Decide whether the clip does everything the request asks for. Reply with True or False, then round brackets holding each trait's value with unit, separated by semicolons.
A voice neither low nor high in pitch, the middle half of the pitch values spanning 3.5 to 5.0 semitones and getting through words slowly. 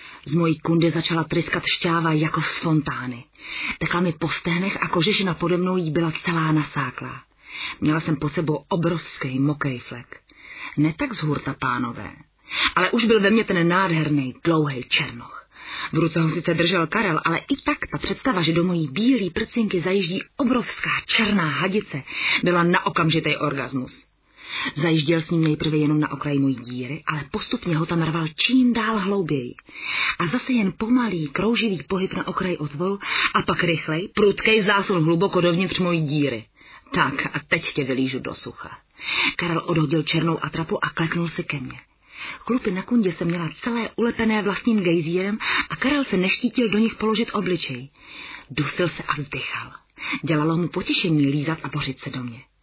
False (170 Hz; 4.5 semitones; 170 wpm)